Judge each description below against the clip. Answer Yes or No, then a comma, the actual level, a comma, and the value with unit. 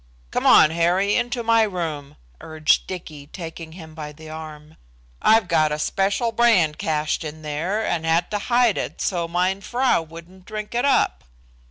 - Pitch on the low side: No, medium, 170 Hz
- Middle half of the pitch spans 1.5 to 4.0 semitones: No, average, 4.8 semitones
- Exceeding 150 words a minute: Yes, average, 170 wpm